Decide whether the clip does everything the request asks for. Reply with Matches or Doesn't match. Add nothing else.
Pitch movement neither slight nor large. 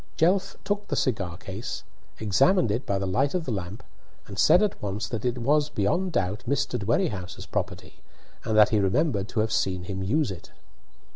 Doesn't match